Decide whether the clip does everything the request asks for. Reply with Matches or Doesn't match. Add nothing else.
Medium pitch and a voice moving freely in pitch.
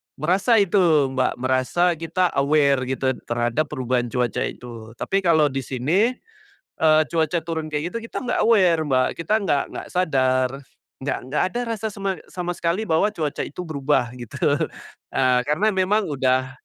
Matches